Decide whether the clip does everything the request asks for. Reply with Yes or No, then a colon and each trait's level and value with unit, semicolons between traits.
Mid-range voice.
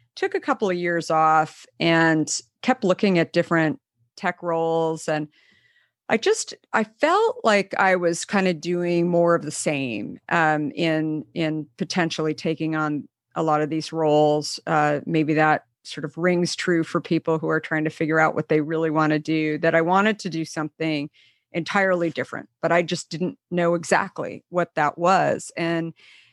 Yes: medium, 165 Hz